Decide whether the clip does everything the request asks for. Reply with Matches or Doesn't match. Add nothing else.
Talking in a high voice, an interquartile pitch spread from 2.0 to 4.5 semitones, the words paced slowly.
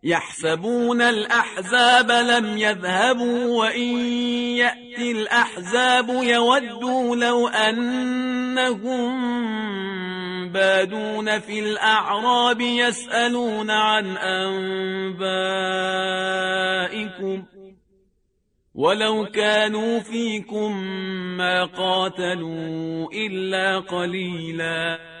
Matches